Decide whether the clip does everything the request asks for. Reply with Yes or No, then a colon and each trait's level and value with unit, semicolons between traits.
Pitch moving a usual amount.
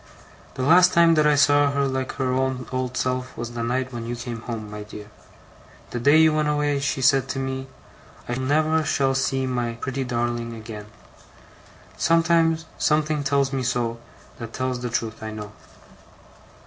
Yes: average, 3.4 semitones